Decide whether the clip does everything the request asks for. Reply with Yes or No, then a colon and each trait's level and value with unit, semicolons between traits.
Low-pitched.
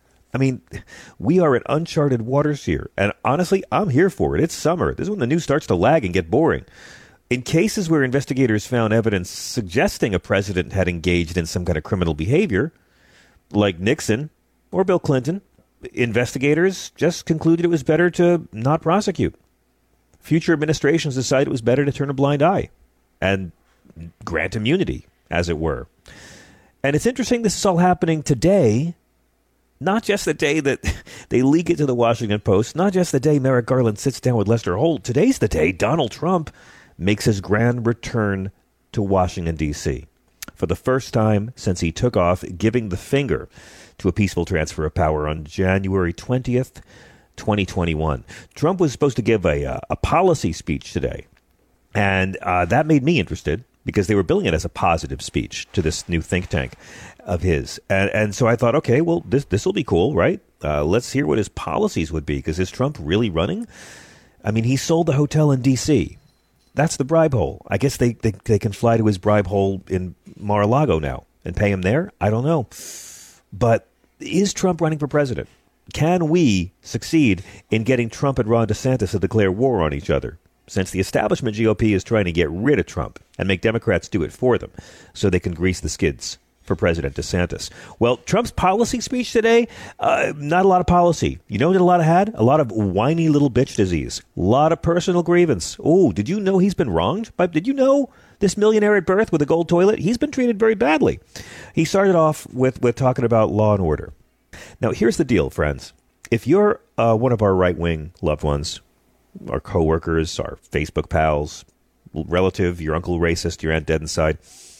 Yes: low, 115 Hz